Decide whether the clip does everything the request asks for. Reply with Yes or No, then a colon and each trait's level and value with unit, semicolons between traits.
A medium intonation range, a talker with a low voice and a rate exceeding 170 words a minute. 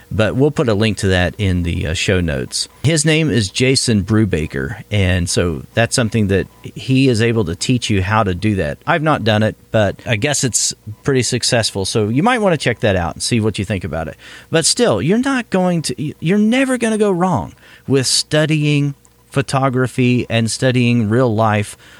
No: wide, 5.7 semitones; low, 115 Hz; fast, 205 wpm